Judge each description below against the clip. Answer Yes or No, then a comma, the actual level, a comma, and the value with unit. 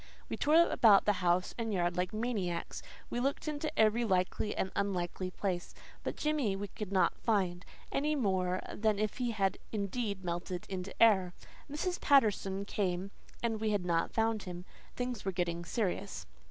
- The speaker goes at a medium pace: Yes, average, 165 wpm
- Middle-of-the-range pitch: No, high, 200 Hz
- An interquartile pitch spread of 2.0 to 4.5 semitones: Yes, average, 3.8 semitones